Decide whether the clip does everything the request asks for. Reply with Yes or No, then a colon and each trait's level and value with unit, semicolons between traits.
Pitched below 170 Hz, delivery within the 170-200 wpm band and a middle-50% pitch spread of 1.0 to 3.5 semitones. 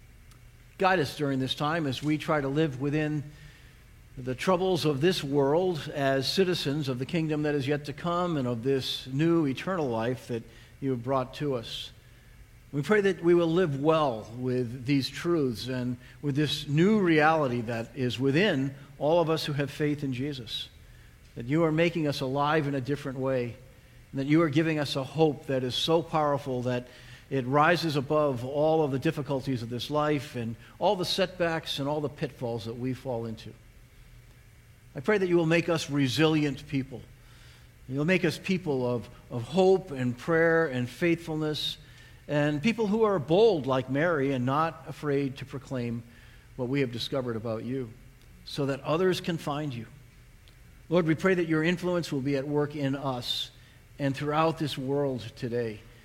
No: medium, 140 Hz; average, 180 wpm; average, 3.9 semitones